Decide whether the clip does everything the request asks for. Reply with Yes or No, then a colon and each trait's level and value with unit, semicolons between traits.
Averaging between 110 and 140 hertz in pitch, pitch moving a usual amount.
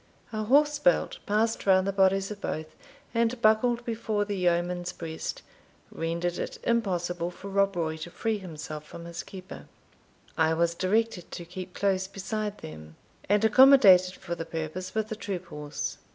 No: medium, 185 Hz; average, 4.0 semitones